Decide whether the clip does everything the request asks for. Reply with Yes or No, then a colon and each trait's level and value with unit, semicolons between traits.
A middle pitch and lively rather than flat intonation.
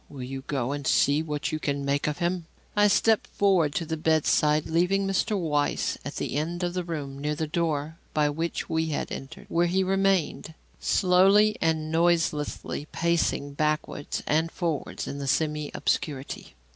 No: medium, 160 Hz; average, 3.0 semitones